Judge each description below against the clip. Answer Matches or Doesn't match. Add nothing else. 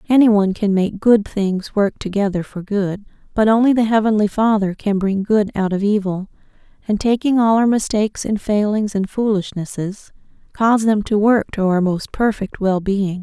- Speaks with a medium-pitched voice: Doesn't match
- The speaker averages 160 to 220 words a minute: Matches